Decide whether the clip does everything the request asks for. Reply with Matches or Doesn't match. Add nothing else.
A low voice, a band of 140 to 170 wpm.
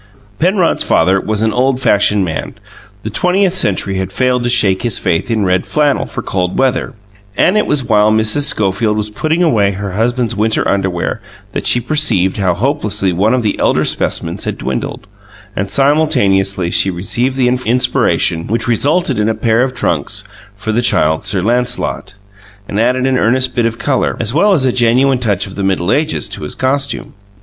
Doesn't match